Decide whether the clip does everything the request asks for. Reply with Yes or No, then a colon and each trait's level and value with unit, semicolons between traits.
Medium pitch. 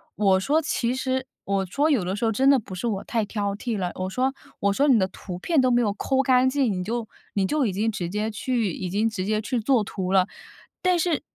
No: high, 220 Hz